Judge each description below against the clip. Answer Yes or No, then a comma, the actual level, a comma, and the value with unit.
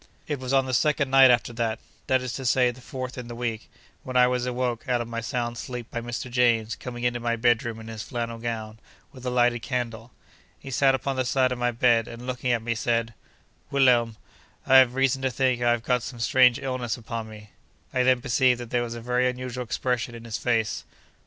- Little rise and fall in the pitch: Yes, narrow, 1.6 semitones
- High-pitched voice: No, low, 120 Hz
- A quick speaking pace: Yes, fast, 225 wpm